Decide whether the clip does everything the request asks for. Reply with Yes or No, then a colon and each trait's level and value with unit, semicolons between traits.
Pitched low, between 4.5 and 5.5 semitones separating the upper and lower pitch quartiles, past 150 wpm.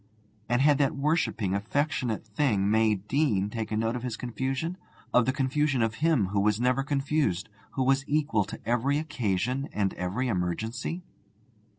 Yes: low, 125 Hz; average, 4.8 semitones; average, 160 wpm